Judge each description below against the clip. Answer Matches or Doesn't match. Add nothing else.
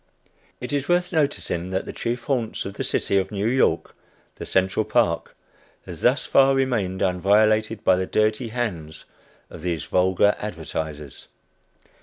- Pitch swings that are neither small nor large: Matches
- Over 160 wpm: Doesn't match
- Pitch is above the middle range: Doesn't match